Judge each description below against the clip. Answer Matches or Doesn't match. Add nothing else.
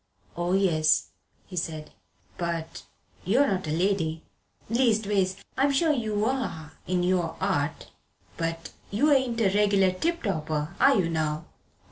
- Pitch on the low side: Doesn't match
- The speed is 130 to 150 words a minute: Matches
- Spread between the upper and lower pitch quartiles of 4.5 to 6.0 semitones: Matches